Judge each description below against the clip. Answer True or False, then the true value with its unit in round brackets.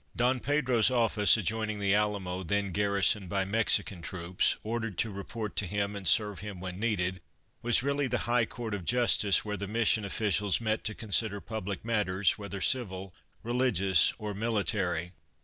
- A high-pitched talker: False (105 Hz)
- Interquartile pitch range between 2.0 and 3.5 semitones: True (2.7 semitones)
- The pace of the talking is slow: False (165 wpm)